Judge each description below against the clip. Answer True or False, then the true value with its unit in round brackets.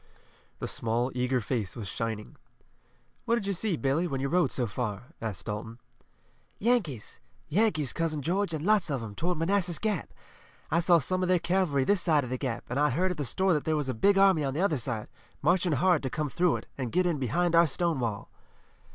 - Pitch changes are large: True (6.1 semitones)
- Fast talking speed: True (215 wpm)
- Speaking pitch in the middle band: True (155 Hz)